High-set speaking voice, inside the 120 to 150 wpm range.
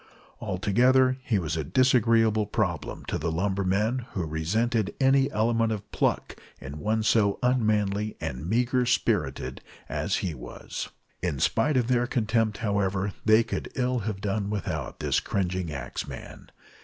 No: low, 105 Hz; average, 145 wpm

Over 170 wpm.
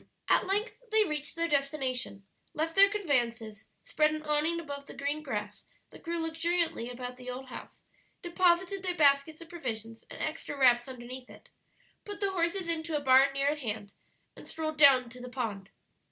Yes: average, 180 wpm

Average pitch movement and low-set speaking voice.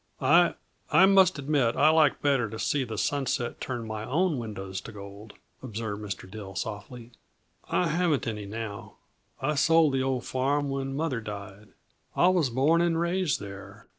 No: wide, 6.2 semitones; low, 130 Hz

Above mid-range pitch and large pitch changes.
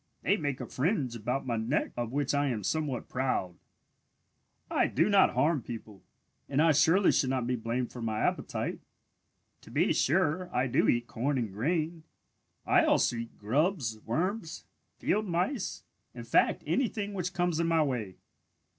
No: medium, 140 Hz; wide, 6.1 semitones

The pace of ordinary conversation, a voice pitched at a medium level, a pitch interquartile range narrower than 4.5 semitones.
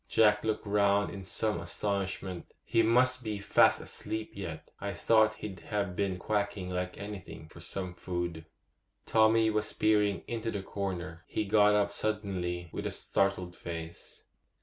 No: average, 150 wpm; low, 100 Hz; average, 2.9 semitones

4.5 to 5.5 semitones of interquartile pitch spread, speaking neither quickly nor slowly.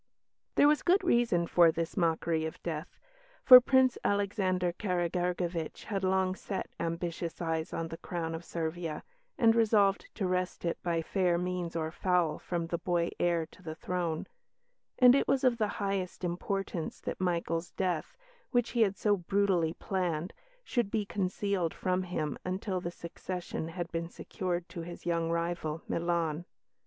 No: average, 2.7 semitones; average, 160 wpm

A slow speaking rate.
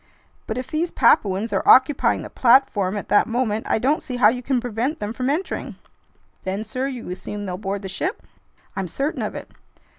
No: average, 200 wpm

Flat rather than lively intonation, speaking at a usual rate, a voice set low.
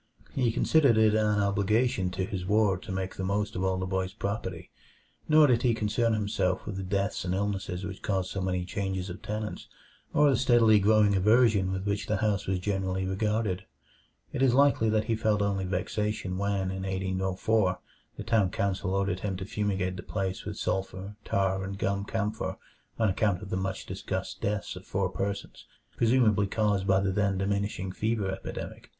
Yes: narrow, 2.2 semitones; average, 185 wpm; low, 100 Hz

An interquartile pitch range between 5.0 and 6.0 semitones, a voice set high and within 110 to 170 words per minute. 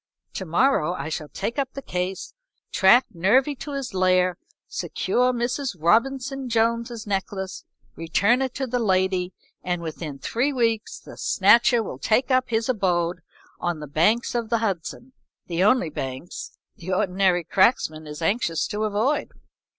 Yes: wide, 5.5 semitones; high, 205 Hz; average, 150 wpm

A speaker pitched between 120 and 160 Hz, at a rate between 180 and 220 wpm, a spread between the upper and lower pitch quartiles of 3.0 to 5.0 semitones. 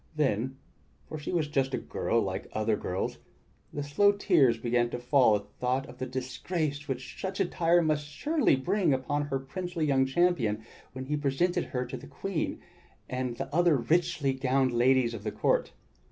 Yes: low, 135 Hz; average, 185 wpm; average, 4.1 semitones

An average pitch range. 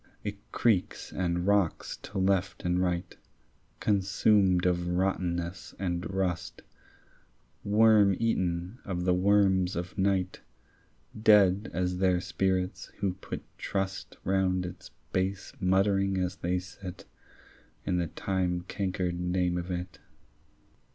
No: narrow, 1.5 semitones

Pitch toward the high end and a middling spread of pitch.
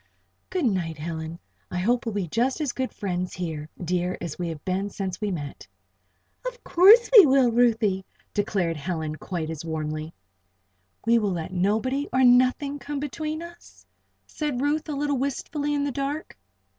No: high, 220 Hz; wide, 8.2 semitones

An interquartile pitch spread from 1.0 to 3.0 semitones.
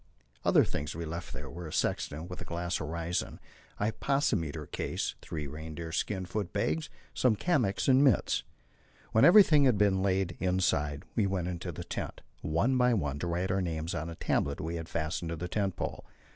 No: average, 4.3 semitones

